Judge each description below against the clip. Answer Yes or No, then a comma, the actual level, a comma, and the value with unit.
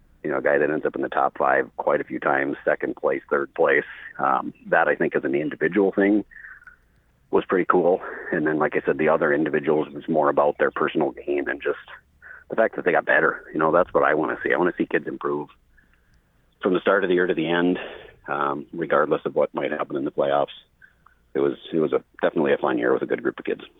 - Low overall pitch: Yes, low, 105 Hz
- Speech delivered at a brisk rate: Yes, fast, 250 wpm